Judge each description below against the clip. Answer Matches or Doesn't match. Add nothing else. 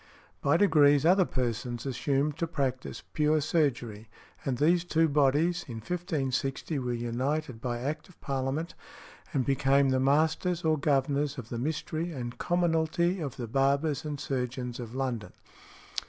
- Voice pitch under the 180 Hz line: Matches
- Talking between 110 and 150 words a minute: Matches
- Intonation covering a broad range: Doesn't match